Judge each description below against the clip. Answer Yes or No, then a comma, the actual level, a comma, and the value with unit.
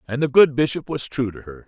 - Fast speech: Yes, fast, 285 wpm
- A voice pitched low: Yes, low, 130 Hz